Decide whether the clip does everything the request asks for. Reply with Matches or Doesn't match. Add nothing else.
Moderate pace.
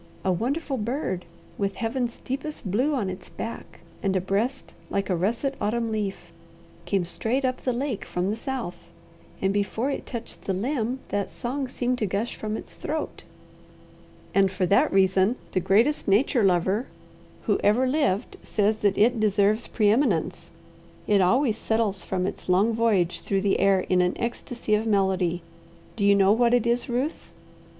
Matches